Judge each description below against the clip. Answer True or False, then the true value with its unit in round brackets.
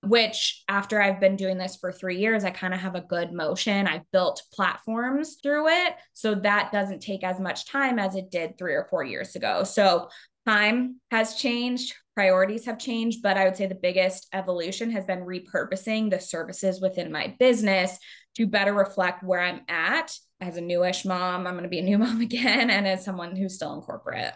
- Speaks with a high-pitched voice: True (195 Hz)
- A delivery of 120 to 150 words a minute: False (205 wpm)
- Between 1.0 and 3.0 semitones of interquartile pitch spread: False (3.4 semitones)